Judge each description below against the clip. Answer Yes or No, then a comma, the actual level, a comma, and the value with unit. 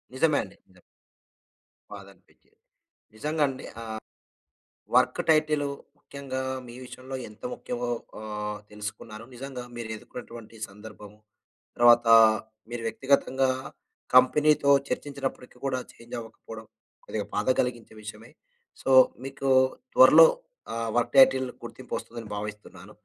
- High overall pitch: No, low, 120 Hz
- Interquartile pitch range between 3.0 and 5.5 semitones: Yes, average, 3.7 semitones